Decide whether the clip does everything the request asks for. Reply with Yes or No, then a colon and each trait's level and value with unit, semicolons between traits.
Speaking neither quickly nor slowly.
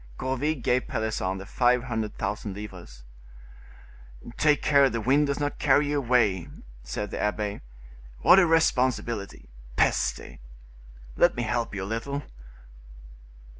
No: slow, 130 wpm